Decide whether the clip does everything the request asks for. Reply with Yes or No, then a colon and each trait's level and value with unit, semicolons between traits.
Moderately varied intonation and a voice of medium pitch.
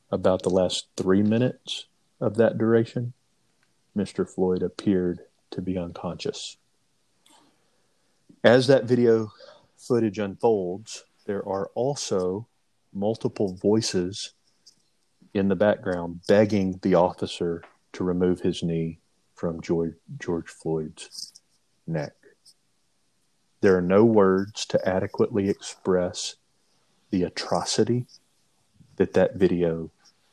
No: average, 3.9 semitones; very low, 95 Hz